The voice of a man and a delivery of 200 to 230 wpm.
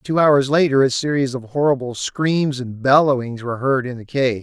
Yes: male; fast, 205 wpm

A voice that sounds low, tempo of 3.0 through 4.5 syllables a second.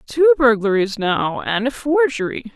No: high, 225 Hz; 4.4 syllables/s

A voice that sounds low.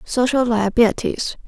No: high, 235 Hz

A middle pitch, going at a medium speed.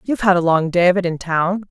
No: medium, 180 Hz; fast, 315 wpm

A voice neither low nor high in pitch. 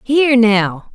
No: high, 235 Hz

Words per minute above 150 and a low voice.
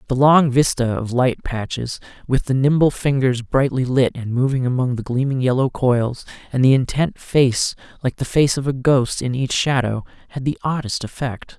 Yes: average, 185 wpm; low, 130 Hz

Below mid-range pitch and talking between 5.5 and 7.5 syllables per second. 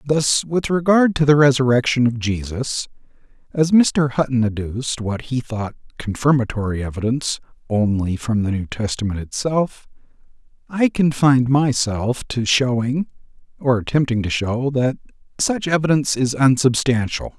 No: low, 125 Hz; 4.7 syllables/s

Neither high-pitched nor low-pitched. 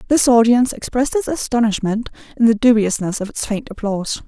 No: high, 230 Hz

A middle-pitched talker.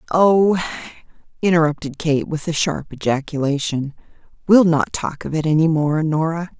Yes: medium, 160 Hz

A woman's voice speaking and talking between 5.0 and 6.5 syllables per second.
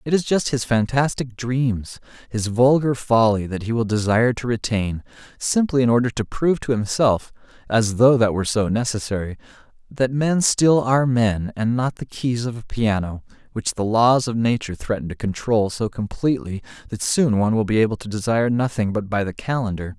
No: male; 5.3 syllables/s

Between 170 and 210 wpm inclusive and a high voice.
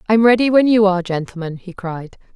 Yes: fast, 205 wpm; high, 195 Hz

